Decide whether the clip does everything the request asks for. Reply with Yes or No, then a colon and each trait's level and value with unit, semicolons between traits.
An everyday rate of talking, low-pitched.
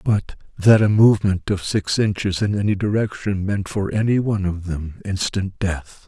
Yes: average, 170 wpm; low, 100 Hz